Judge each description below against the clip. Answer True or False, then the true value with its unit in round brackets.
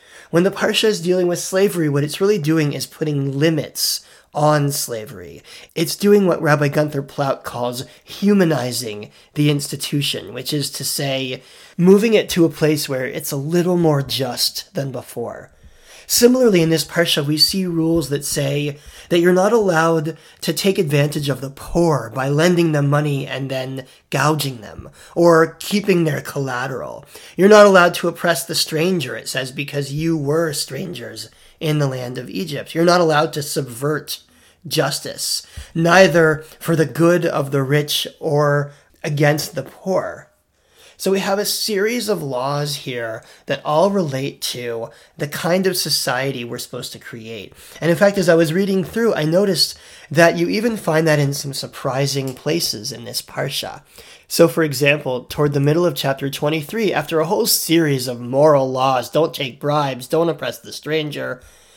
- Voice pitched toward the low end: False (155 Hz)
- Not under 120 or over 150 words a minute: False (170 wpm)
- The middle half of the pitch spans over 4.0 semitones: False (3.7 semitones)